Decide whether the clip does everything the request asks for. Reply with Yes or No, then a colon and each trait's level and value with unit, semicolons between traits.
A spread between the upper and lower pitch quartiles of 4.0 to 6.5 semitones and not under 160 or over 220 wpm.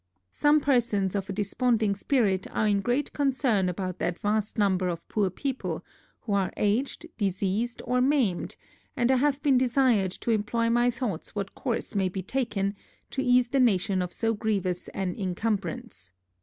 Yes: average, 4.4 semitones; average, 170 wpm